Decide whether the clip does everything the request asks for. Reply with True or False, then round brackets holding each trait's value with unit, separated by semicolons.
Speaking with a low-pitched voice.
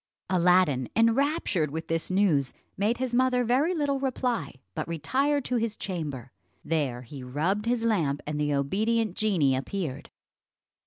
False (190 Hz)